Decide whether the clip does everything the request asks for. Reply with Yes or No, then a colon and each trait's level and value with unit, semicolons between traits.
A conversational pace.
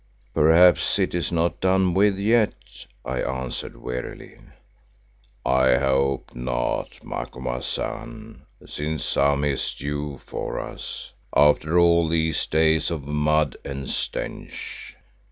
No: slow, 110 wpm